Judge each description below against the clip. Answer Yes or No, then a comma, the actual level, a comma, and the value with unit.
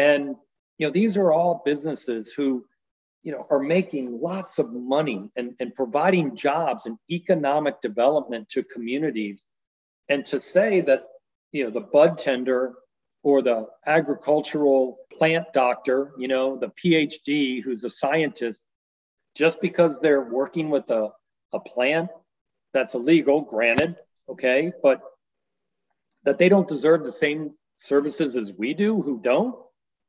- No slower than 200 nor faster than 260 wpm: No, average, 140 wpm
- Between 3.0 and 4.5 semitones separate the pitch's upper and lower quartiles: Yes, average, 4.2 semitones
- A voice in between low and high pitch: Yes, medium, 145 Hz